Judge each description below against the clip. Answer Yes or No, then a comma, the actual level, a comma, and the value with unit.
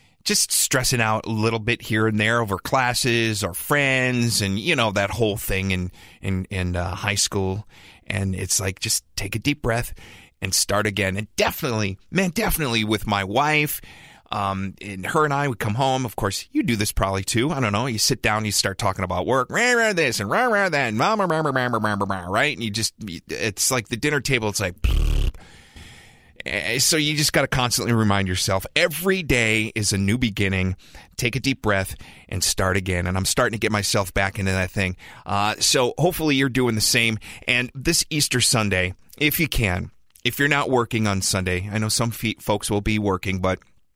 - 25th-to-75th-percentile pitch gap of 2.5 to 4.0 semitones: No, average, 4.8 semitones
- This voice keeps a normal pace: No, fast, 210 wpm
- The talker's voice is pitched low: Yes, low, 110 Hz